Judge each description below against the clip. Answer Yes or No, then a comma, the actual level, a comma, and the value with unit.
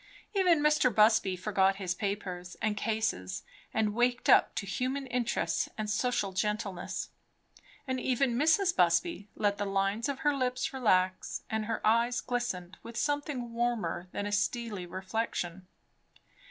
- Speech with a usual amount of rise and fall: Yes, average, 4.3 semitones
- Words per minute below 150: Yes, average, 140 wpm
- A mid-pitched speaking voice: No, high, 220 Hz